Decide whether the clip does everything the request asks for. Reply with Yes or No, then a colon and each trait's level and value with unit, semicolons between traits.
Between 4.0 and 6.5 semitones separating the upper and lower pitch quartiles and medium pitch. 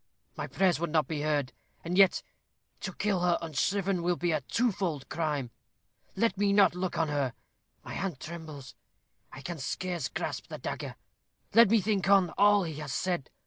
Yes: average, 4.3 semitones; medium, 175 Hz